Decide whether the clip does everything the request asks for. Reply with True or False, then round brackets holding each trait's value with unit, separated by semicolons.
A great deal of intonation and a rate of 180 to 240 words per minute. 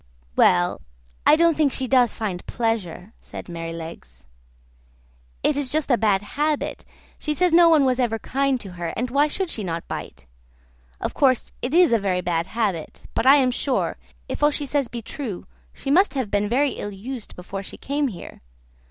True (6.7 semitones; 190 wpm)